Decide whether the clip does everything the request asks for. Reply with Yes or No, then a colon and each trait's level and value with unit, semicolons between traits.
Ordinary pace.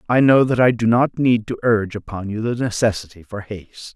No: fast, 230 wpm